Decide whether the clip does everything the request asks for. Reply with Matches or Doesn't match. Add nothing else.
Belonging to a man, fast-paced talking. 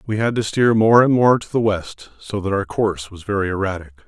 Matches